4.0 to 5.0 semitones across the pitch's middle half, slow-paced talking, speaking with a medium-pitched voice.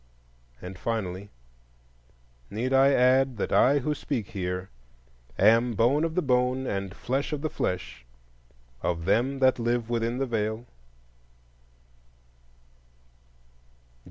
No: average, 4.7 semitones; slow, 115 wpm; low, 120 Hz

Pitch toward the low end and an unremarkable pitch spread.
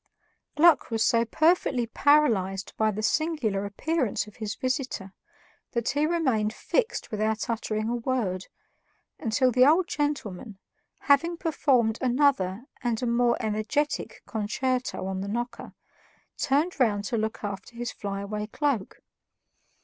No: high, 235 Hz; average, 4.9 semitones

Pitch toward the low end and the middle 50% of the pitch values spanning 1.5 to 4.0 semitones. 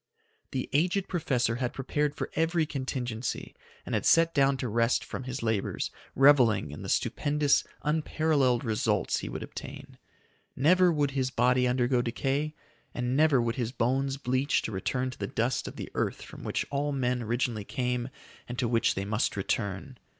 Yes: low, 130 Hz; average, 3.2 semitones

